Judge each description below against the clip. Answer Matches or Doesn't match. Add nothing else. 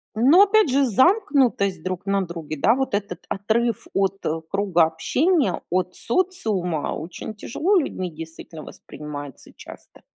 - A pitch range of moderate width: Doesn't match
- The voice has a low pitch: Doesn't match